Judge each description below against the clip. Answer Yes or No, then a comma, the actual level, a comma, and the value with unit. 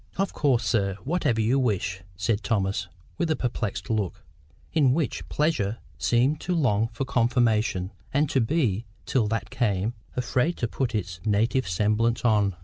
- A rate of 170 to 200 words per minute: No, average, 155 wpm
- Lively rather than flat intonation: No, average, 4.3 semitones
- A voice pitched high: No, low, 115 Hz